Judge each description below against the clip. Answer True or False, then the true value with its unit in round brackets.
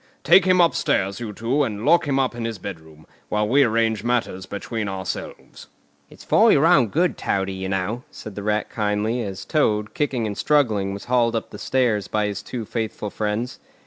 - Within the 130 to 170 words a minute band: False (195 wpm)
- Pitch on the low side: True (110 Hz)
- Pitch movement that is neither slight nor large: True (3.4 semitones)